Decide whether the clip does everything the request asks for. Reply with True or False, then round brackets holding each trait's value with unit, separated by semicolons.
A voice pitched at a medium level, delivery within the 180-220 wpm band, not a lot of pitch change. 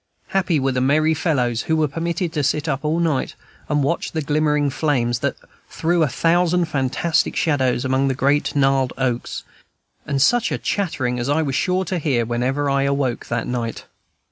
False (145 Hz; 185 wpm; 3.4 semitones)